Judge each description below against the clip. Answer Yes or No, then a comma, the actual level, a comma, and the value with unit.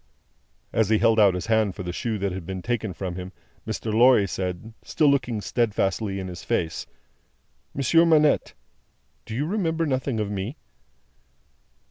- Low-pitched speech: Yes, low, 110 Hz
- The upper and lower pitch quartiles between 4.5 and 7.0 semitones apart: Yes, average, 5.2 semitones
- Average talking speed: Yes, average, 160 wpm